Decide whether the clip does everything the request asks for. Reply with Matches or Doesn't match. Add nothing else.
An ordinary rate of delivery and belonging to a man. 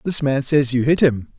Doesn't match